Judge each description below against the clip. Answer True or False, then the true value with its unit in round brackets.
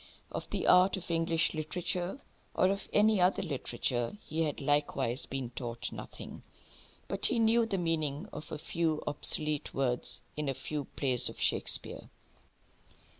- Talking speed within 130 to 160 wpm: True (150 wpm)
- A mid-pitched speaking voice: True (155 Hz)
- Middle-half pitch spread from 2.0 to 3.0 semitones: False (4.9 semitones)